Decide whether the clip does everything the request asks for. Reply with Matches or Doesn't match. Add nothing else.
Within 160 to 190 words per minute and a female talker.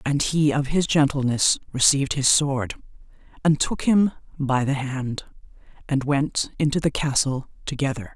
Doesn't match